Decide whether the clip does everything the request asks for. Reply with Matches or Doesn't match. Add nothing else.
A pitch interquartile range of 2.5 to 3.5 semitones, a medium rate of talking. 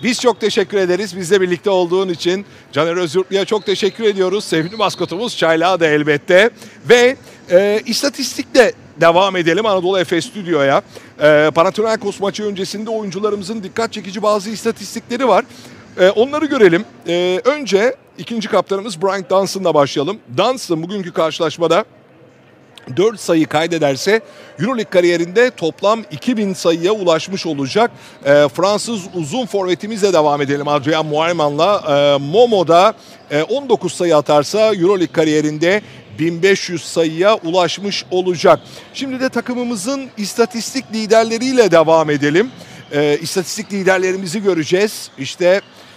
Doesn't match